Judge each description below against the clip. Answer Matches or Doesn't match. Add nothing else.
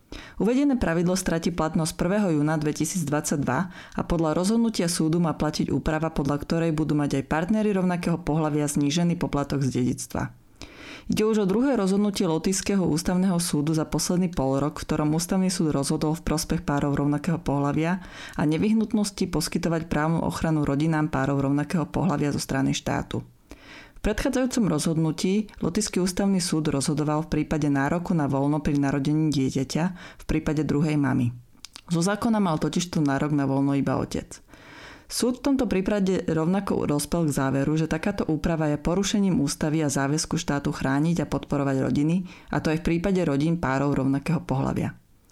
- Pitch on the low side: Doesn't match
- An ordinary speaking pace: Matches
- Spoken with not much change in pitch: Doesn't match